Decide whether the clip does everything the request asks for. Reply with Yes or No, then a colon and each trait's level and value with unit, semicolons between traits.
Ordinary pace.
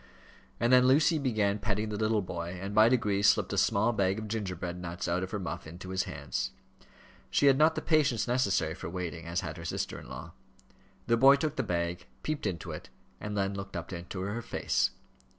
No: fast, 210 wpm